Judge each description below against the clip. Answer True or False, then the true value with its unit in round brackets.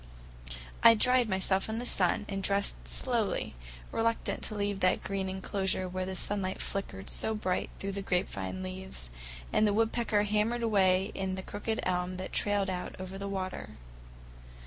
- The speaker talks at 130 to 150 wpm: False (165 wpm)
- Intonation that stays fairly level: True (2.1 semitones)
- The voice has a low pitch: False (195 Hz)